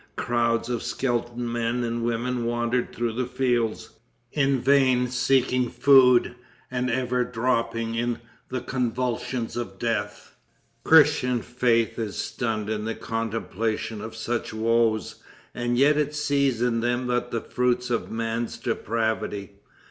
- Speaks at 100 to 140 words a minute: Yes, slow, 135 wpm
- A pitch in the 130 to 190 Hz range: No, low, 120 Hz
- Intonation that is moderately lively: No, narrow, 1.6 semitones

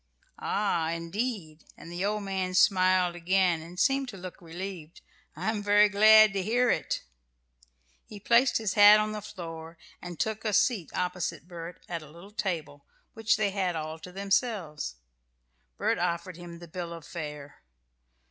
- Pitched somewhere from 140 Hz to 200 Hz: Yes, medium, 185 Hz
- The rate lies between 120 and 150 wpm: No, average, 160 wpm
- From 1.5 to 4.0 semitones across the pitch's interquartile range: Yes, average, 3.7 semitones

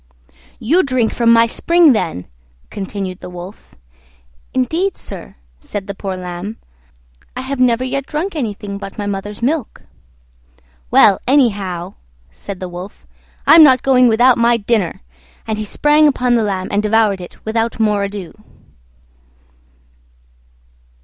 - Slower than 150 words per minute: Yes, slow, 135 wpm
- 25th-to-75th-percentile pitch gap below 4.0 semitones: No, average, 4.5 semitones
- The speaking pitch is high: Yes, high, 220 Hz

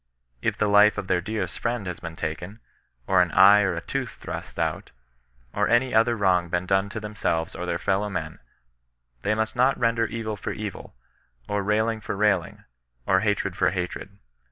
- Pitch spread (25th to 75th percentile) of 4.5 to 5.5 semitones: No, average, 3.3 semitones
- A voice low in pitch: Yes, low, 100 Hz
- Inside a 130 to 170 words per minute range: No, average, 185 wpm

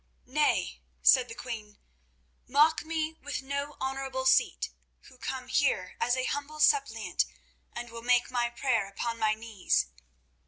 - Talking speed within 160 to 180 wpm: No, average, 145 wpm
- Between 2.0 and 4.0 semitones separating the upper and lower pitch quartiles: Yes, average, 3.5 semitones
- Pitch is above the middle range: Yes, very high, 255 Hz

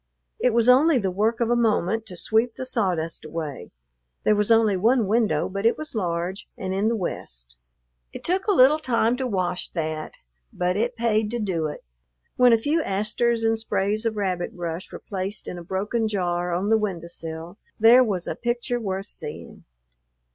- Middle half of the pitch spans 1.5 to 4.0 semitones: No, average, 4.5 semitones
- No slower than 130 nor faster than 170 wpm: No, average, 190 wpm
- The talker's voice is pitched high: Yes, high, 210 Hz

